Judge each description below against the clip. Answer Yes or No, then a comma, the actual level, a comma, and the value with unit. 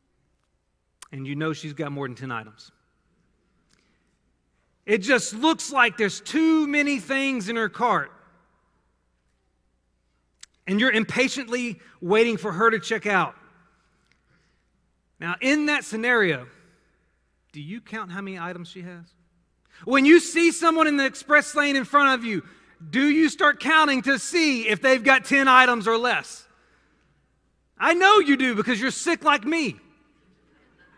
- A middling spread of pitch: No, wide, 7.8 semitones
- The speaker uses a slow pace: No, average, 145 wpm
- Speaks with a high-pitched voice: Yes, high, 240 Hz